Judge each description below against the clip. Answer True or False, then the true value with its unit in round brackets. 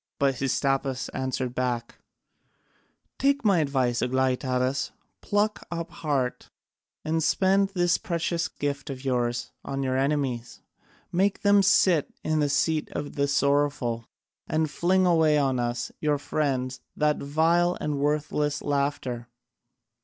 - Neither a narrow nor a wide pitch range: True (3.8 semitones)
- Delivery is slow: True (125 wpm)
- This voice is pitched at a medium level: True (145 Hz)